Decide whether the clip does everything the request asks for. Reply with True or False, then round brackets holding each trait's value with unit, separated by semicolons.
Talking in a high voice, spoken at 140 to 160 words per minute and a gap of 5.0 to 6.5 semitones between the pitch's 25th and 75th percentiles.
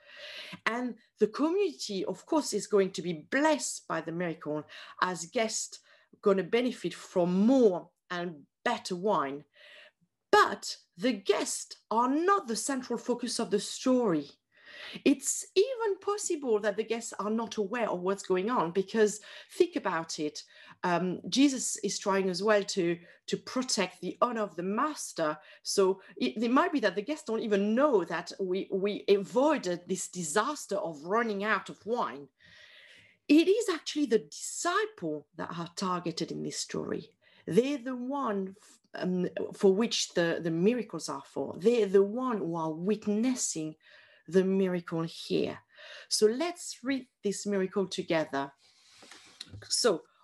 True (210 Hz; 150 wpm; 5.6 semitones)